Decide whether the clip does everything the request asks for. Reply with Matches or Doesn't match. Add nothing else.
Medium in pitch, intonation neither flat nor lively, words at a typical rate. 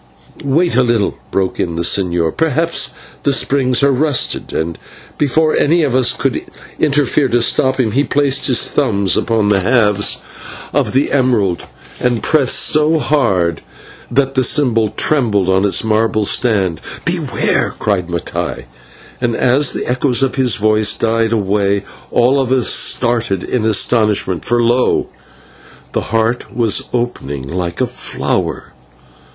Doesn't match